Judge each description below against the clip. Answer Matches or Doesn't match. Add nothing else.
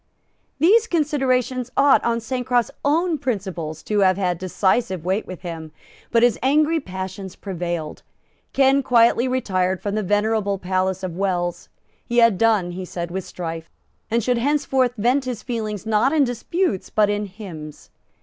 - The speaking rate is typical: Matches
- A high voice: Matches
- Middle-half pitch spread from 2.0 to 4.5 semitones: Doesn't match